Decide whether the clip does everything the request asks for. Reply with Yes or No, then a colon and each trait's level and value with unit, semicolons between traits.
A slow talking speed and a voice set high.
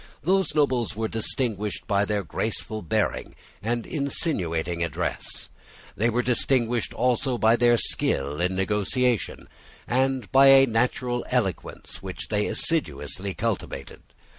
No: slow, 120 wpm; low, 115 Hz